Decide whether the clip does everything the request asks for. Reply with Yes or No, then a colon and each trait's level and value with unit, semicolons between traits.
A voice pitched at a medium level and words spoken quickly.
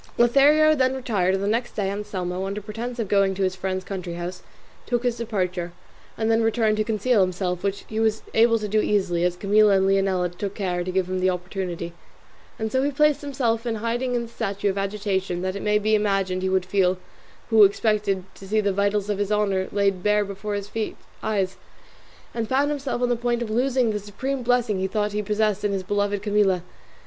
No: high, 205 Hz; fast, 215 wpm